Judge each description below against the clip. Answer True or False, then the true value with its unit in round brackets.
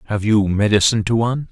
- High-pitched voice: False (105 Hz)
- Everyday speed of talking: True (160 wpm)